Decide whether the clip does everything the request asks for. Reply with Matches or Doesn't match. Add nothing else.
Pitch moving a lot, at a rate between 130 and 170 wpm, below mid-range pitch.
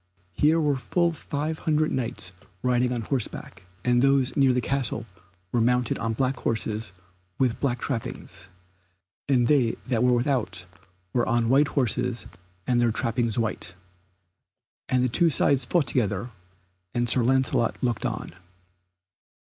Doesn't match